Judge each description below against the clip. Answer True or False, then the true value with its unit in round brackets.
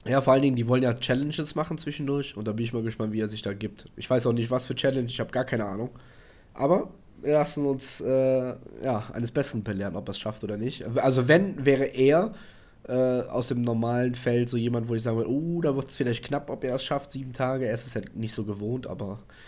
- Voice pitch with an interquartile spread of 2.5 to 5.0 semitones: True (3.0 semitones)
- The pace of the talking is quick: True (255 wpm)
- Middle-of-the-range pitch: False (125 Hz)